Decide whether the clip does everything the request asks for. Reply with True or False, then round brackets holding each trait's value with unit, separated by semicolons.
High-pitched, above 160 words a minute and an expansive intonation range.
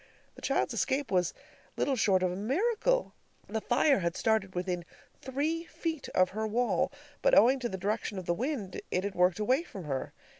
True (220 Hz; 190 wpm; 6.8 semitones)